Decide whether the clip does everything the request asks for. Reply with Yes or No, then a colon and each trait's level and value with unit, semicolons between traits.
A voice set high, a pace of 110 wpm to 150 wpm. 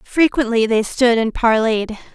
Yes: high, 235 Hz; average, 140 wpm